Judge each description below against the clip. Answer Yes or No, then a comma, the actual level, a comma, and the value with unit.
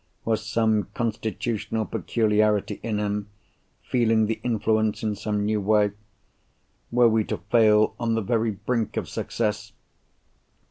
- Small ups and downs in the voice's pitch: Yes, narrow, 1.3 semitones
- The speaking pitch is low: Yes, low, 110 Hz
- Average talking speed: No, slow, 130 wpm